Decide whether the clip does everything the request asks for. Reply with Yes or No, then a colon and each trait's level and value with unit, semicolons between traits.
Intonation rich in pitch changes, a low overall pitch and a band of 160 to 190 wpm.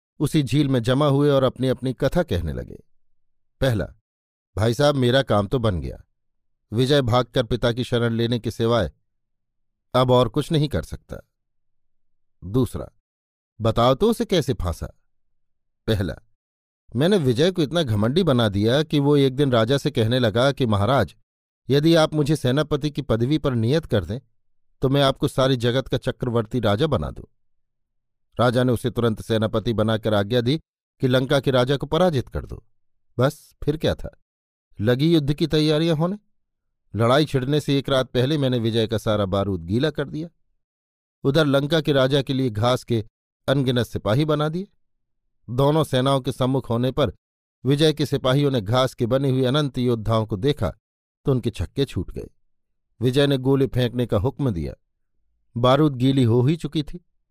No: average, 4.2 semitones; low, 125 Hz; average, 170 wpm